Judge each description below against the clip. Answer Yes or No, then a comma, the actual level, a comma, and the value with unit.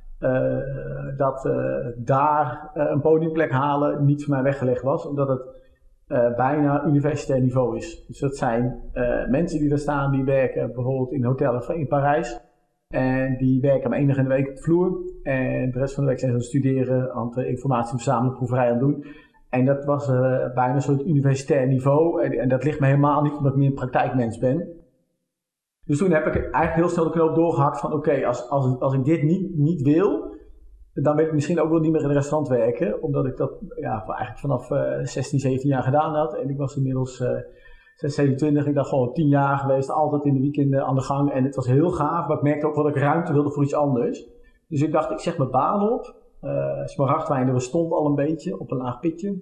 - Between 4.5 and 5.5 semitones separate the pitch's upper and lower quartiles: No, average, 2.7 semitones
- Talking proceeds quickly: Yes, fast, 225 wpm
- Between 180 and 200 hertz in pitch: No, medium, 140 Hz